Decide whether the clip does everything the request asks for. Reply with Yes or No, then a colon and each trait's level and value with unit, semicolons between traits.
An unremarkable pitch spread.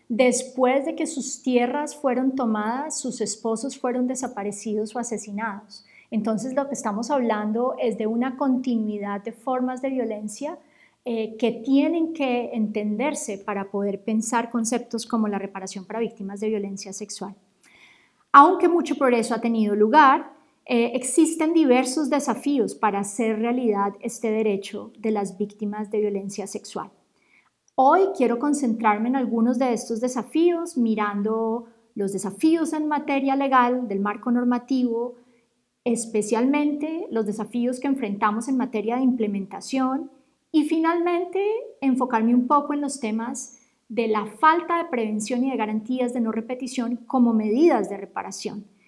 Yes: average, 3.8 semitones